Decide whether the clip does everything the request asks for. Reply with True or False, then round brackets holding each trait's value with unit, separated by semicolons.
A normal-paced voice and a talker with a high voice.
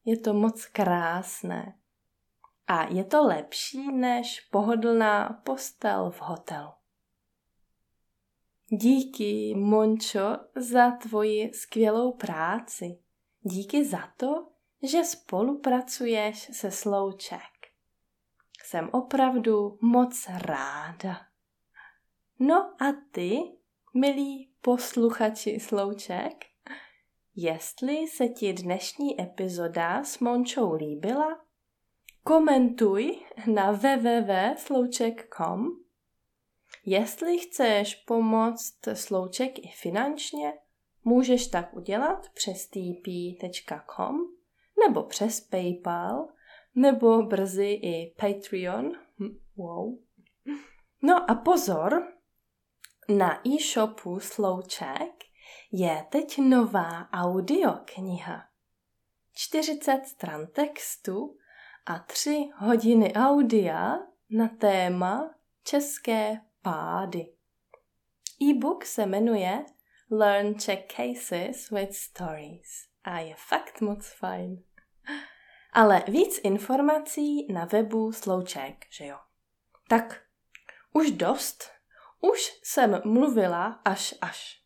False (85 wpm; 225 Hz)